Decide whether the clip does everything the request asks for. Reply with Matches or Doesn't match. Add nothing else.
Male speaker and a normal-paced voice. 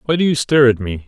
Doesn't match